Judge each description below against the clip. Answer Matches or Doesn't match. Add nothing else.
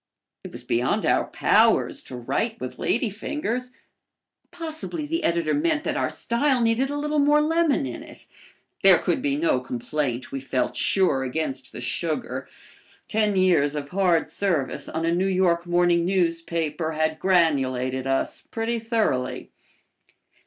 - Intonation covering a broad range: Matches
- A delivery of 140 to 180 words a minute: Matches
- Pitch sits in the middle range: Matches